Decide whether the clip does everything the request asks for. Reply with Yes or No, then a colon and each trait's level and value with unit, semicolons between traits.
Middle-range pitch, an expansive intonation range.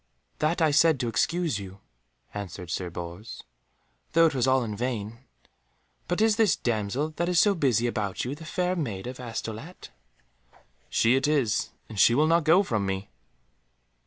No: low, 125 Hz; wide, 7.4 semitones